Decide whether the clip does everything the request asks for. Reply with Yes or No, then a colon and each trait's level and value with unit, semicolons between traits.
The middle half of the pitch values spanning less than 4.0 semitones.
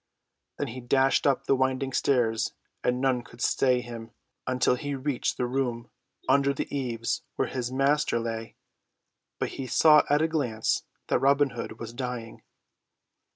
Yes: narrow, 2.5 semitones